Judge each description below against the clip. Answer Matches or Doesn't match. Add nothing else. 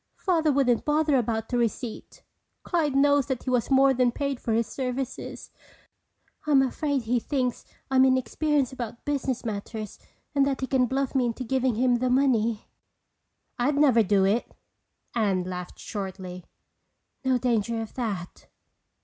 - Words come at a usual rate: Matches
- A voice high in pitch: Matches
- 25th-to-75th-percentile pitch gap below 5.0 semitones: Matches